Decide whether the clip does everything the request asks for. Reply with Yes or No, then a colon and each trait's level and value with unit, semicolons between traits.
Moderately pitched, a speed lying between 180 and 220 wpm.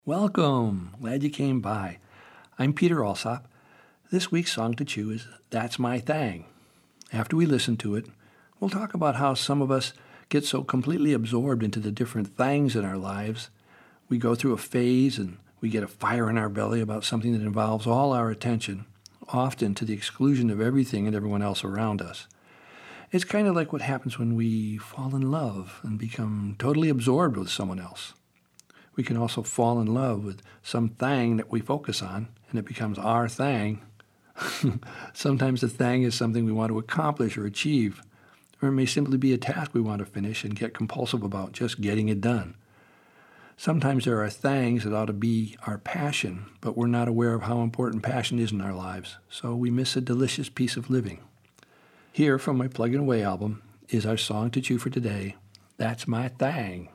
No: low, 115 Hz; average, 195 wpm